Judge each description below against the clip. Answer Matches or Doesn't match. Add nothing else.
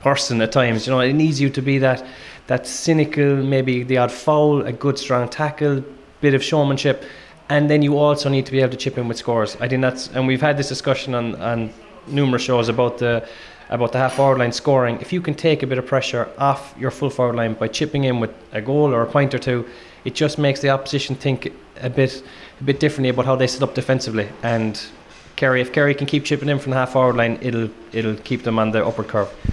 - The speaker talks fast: Matches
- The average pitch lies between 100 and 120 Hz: Doesn't match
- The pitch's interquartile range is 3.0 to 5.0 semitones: Doesn't match